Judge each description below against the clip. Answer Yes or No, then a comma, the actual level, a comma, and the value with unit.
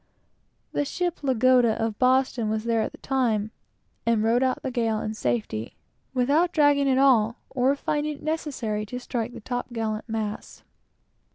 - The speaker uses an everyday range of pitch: Yes, average, 3.6 semitones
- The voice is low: No, high, 245 Hz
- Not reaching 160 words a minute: No, average, 165 wpm